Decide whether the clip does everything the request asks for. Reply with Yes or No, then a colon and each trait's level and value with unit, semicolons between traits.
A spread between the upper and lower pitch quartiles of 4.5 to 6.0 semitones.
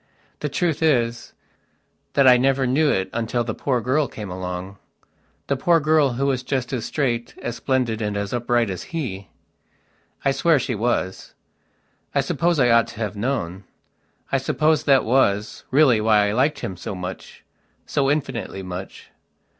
Yes: average, 4.8 semitones